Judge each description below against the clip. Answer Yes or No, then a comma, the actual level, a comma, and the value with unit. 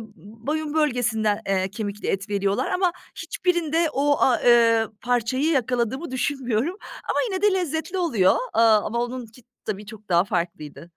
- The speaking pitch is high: Yes, high, 240 Hz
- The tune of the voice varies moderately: No, wide, 6.2 semitones